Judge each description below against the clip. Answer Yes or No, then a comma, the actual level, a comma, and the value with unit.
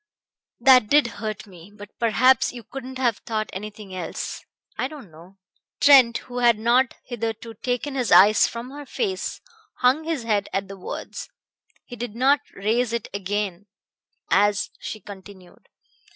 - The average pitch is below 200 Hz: No, high, 230 Hz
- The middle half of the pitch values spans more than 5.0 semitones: No, average, 3.8 semitones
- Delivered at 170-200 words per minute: No, average, 150 wpm